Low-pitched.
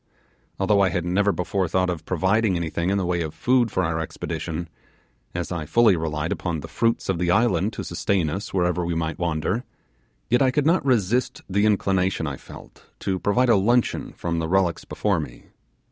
Yes: very low, 95 Hz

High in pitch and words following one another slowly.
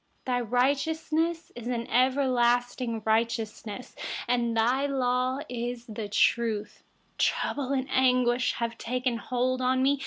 Yes: high, 245 Hz; slow, 105 wpm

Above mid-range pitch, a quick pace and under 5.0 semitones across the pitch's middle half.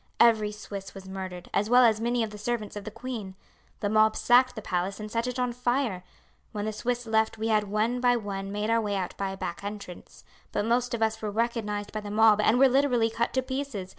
Yes: high, 220 Hz; fast, 240 wpm; average, 2.7 semitones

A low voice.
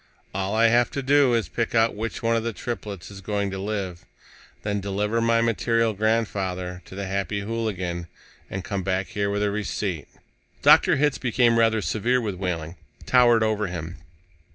Yes: low, 105 Hz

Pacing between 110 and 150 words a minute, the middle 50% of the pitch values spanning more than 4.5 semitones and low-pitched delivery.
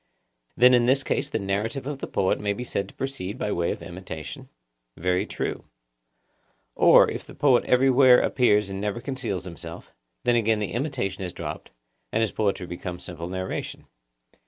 No: average, 175 wpm; average, 5.0 semitones; low, 105 Hz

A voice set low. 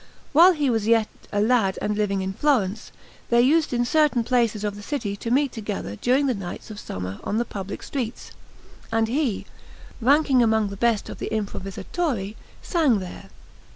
No: high, 225 Hz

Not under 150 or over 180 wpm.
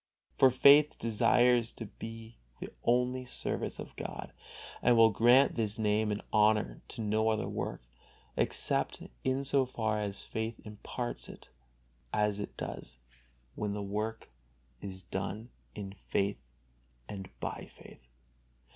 No: slow, 135 wpm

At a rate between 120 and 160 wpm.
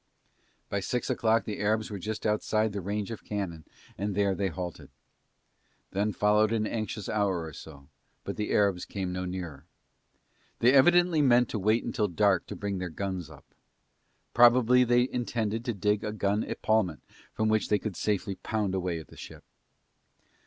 No: average, 175 wpm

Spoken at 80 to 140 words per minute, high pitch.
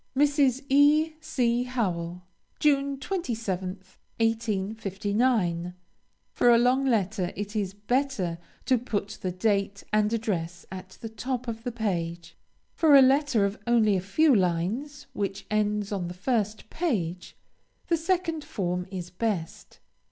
Yes: slow, 135 wpm; high, 215 Hz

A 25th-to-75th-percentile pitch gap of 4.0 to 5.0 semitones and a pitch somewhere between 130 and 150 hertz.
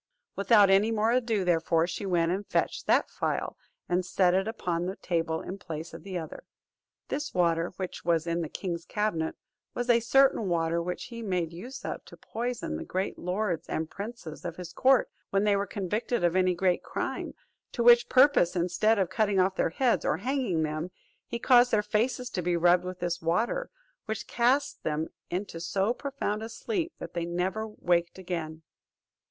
No: average, 4.7 semitones; high, 190 Hz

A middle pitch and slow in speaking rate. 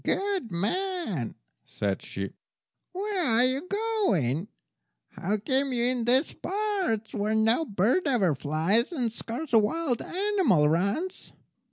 No: high, 240 Hz; slow, 130 wpm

